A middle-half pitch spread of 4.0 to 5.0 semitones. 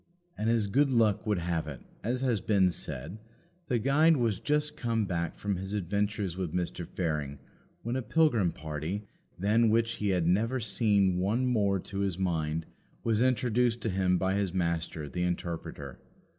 Yes: average, 4.7 semitones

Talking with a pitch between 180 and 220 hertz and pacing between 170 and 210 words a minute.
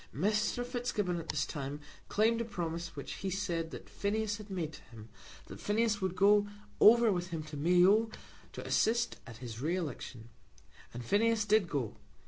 Yes: high, 190 Hz; average, 175 wpm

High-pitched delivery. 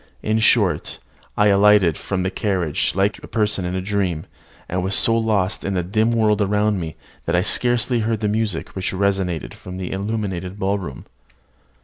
No: low, 100 Hz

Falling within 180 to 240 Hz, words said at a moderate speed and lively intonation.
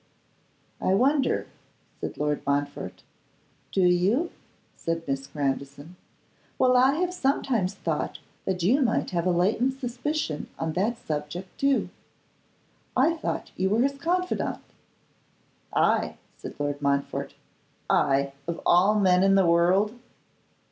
No: high, 190 Hz; slow, 125 wpm; wide, 8.4 semitones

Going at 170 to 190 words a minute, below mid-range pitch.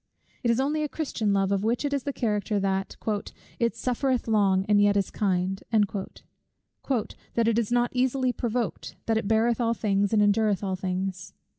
No: average, 180 wpm; high, 220 Hz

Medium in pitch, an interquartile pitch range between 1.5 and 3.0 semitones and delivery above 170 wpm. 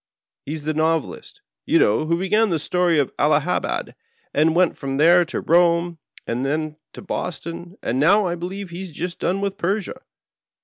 Yes: medium, 170 Hz; average, 2.7 semitones; average, 185 wpm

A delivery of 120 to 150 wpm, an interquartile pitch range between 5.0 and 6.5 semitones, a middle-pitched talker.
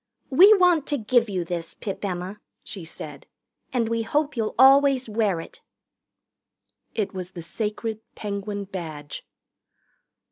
No: slow, 135 wpm; wide, 5.6 semitones; high, 210 Hz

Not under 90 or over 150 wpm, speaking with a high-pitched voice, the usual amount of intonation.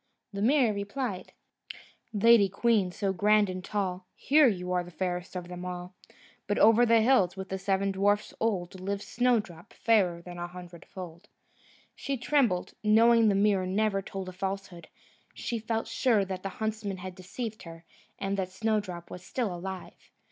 No: average, 160 wpm; high, 195 Hz; average, 3.1 semitones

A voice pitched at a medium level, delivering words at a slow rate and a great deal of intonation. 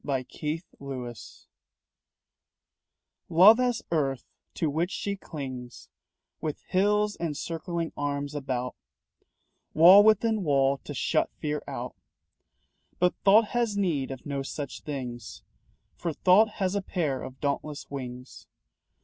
Yes: medium, 150 Hz; slow, 125 wpm; wide, 5.8 semitones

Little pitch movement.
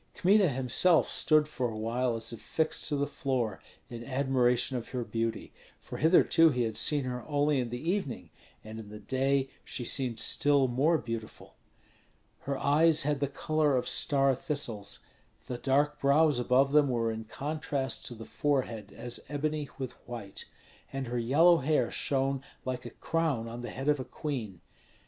No: average, 3.4 semitones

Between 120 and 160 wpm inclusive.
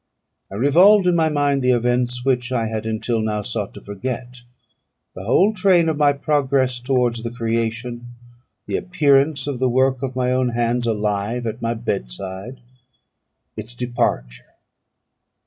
Yes: average, 150 wpm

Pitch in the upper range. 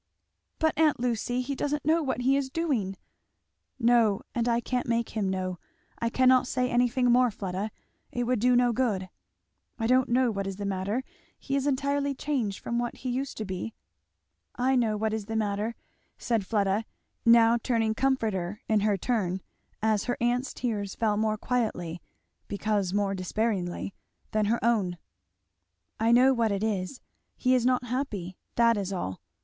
Yes: high, 230 Hz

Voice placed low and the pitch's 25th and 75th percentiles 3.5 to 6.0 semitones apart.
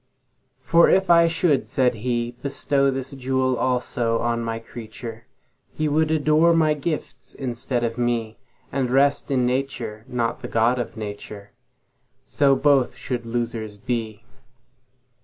No: low, 125 Hz; average, 2.8 semitones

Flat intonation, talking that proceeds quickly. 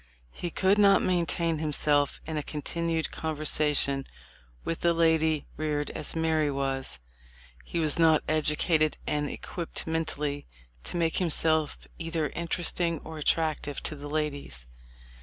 No: narrow, 1.9 semitones; slow, 135 wpm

